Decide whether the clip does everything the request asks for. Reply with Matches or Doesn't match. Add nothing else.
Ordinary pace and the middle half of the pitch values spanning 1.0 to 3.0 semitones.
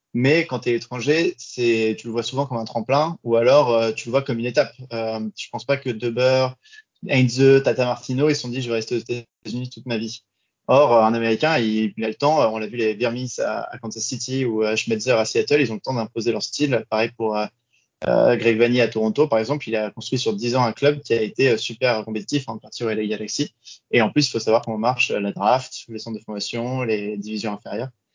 Doesn't match